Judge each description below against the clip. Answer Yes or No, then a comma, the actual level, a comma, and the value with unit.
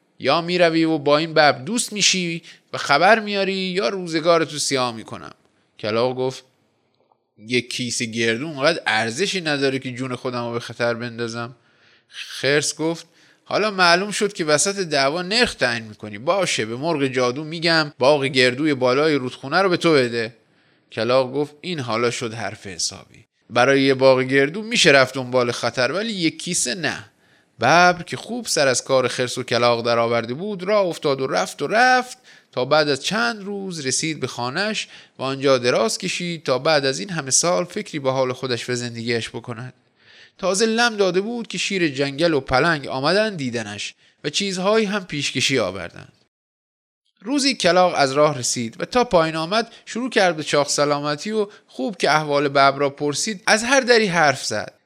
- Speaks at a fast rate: Yes, fast, 175 wpm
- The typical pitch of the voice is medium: Yes, medium, 145 Hz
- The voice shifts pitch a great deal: Yes, wide, 6.6 semitones